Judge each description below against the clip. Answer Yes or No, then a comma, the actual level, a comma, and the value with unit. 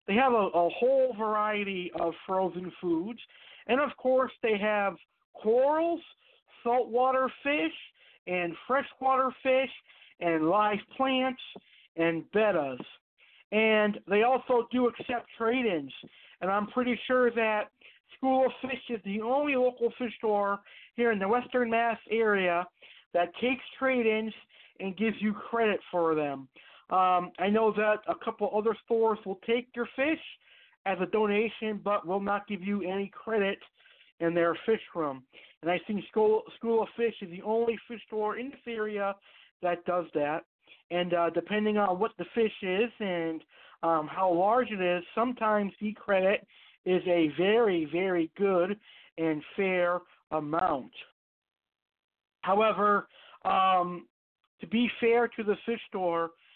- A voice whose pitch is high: Yes, high, 210 Hz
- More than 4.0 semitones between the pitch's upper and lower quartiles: Yes, average, 4.6 semitones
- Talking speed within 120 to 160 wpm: Yes, average, 150 wpm